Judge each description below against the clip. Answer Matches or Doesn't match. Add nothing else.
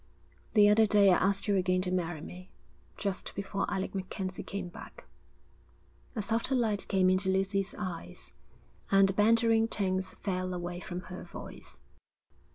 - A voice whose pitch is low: Doesn't match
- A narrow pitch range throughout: Matches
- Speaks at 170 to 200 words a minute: Doesn't match